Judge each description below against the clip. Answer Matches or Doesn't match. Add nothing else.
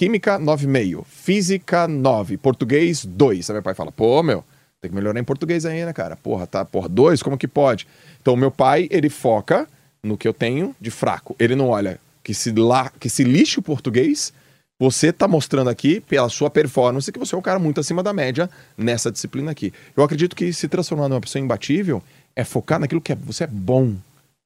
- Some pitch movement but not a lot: Matches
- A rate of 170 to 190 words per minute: Doesn't match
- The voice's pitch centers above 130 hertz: Matches